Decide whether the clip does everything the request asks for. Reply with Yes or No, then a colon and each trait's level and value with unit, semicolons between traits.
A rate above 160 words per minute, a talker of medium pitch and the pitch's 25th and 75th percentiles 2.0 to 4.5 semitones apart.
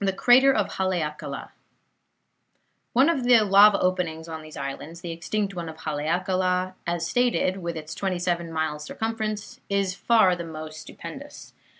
No: average, 140 wpm; medium, 180 Hz; average, 4.2 semitones